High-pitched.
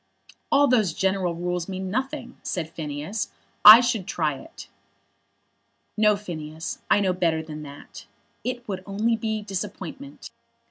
Yes: high, 195 Hz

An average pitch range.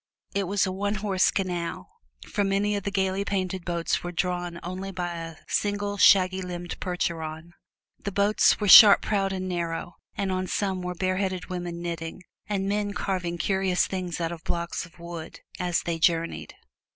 No: narrow, 2.2 semitones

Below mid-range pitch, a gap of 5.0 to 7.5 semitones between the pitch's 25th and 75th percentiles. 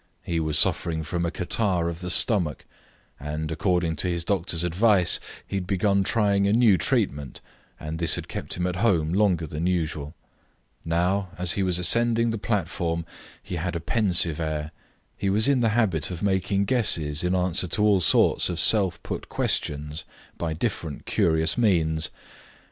No: very low, 90 Hz; average, 3.6 semitones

